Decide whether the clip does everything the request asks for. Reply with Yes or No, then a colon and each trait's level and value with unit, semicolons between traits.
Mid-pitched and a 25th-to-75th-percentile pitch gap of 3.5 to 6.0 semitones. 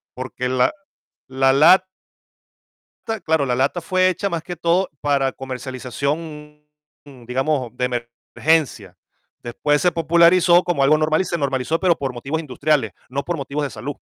Yes: medium, 145 Hz; average, 4.1 semitones